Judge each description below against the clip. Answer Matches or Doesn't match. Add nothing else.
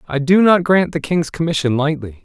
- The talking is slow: Doesn't match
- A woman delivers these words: Doesn't match